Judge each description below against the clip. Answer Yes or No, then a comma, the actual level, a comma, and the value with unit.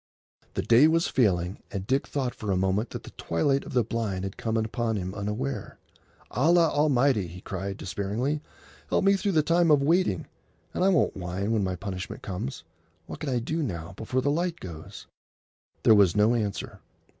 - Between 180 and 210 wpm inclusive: Yes, average, 190 wpm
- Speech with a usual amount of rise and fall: No, wide, 6.8 semitones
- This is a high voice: No, low, 110 Hz